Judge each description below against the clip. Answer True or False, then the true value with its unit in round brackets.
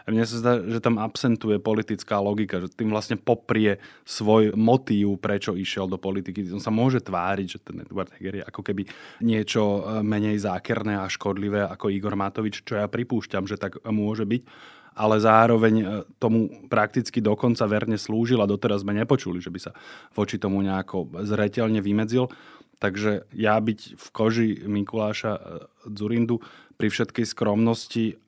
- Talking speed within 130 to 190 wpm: True (155 wpm)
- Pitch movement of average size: False (1.8 semitones)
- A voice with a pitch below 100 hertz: False (105 Hz)